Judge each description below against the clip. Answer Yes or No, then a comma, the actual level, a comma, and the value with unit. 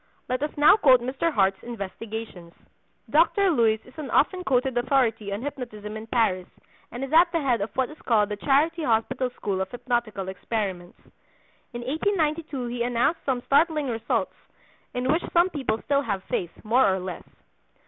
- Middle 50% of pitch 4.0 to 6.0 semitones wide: Yes, average, 5.1 semitones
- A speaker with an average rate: Yes, average, 170 wpm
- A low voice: No, high, 245 Hz